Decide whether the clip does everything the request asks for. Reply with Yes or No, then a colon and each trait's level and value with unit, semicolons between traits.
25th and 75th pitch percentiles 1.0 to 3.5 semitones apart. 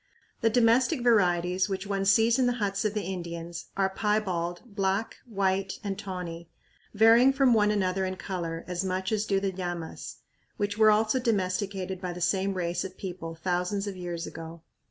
Yes: average, 2.9 semitones